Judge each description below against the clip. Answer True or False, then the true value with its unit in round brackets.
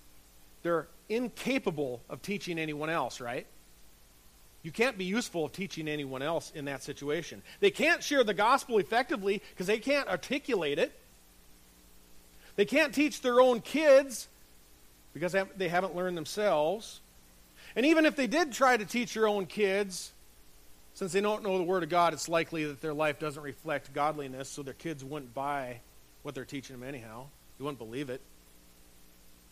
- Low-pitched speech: False (150 Hz)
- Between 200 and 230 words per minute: False (170 wpm)